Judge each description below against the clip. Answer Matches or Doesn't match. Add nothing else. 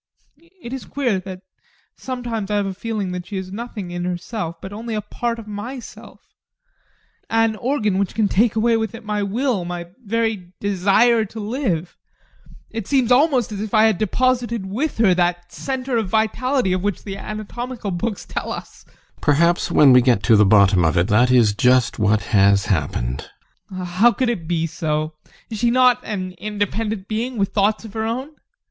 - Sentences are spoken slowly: Doesn't match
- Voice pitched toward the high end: Matches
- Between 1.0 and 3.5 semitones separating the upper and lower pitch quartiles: Doesn't match